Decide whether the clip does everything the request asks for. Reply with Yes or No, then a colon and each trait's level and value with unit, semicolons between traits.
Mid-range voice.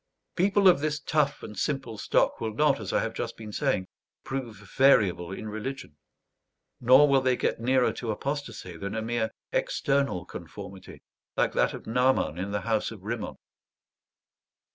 No: low, 115 Hz